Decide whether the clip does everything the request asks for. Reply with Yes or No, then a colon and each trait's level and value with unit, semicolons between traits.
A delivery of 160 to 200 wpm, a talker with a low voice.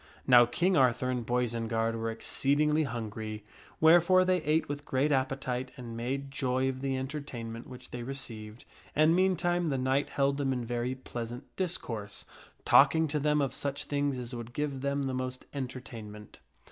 Yes: average, 170 wpm; low, 130 Hz